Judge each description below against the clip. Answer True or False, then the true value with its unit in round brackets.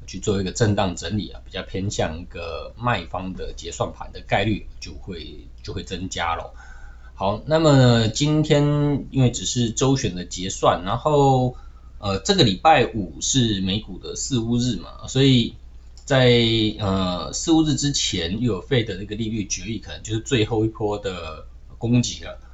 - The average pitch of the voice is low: True (105 Hz)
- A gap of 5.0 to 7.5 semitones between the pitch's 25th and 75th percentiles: True (5.3 semitones)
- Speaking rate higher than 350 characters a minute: False (245 characters per minute)